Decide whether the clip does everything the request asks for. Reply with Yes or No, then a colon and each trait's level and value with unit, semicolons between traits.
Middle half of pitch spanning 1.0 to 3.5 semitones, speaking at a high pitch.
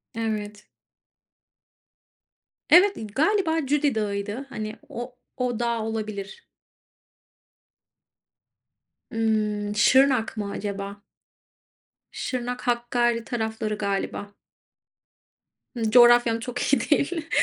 Yes: average, 2.9 semitones; high, 230 Hz